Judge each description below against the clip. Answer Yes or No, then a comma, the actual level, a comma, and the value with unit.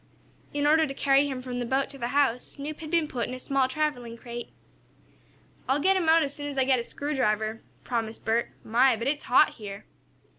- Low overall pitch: No, very high, 265 Hz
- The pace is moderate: No, fast, 220 wpm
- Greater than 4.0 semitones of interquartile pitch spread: No, average, 3.5 semitones